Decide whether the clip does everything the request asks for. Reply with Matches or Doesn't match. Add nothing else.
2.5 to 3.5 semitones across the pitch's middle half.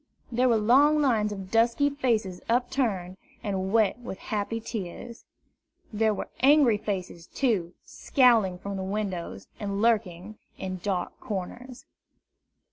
Doesn't match